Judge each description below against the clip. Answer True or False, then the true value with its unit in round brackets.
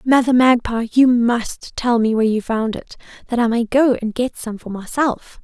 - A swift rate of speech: True (210 wpm)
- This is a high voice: True (235 Hz)